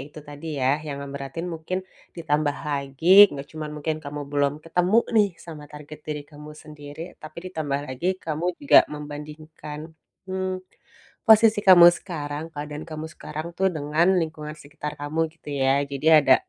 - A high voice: No, medium, 150 Hz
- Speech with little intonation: Yes, narrow, 2.1 semitones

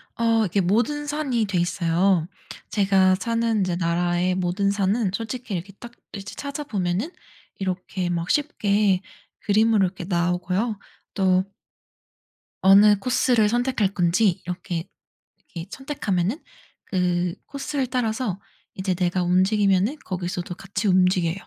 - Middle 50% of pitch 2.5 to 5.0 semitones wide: Yes, average, 3.8 semitones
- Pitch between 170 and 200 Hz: Yes, high, 195 Hz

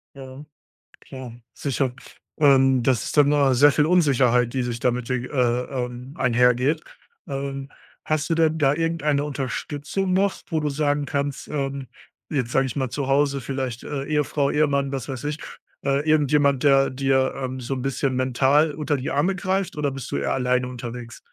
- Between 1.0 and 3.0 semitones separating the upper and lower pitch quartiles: Yes, narrow, 2.4 semitones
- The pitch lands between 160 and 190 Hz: No, low, 135 Hz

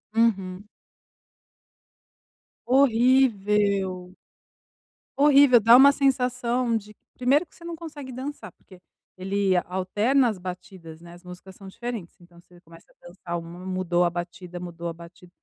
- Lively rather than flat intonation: Yes, wide, 5.8 semitones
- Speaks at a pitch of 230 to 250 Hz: No, high, 195 Hz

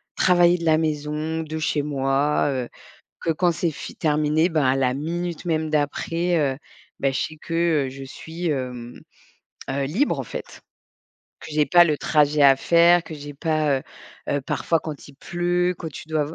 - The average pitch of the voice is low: No, medium, 155 Hz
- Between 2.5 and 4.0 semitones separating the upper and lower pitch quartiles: Yes, average, 2.8 semitones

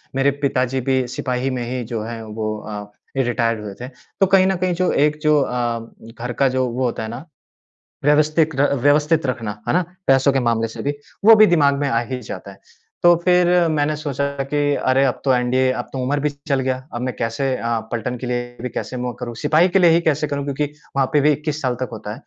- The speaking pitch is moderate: No, low, 130 Hz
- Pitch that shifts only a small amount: No, average, 3.4 semitones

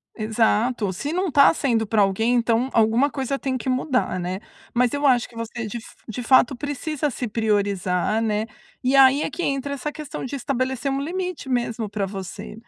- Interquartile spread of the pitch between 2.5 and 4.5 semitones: Yes, average, 3.9 semitones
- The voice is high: Yes, high, 245 Hz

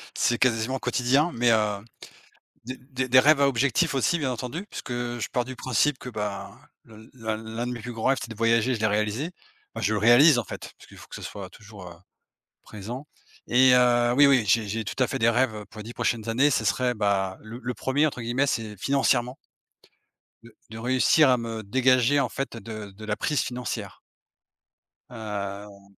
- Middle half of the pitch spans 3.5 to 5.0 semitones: No, average, 3.1 semitones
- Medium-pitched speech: No, low, 120 Hz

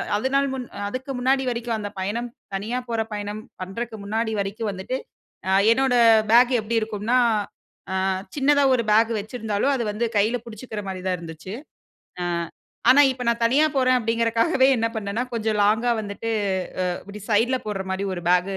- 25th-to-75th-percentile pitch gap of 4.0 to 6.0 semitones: No, average, 3.3 semitones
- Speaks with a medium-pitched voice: No, high, 225 Hz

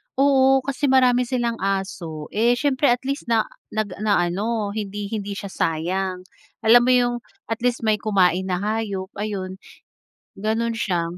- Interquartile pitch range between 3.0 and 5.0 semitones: Yes, average, 4.0 semitones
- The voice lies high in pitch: Yes, high, 215 Hz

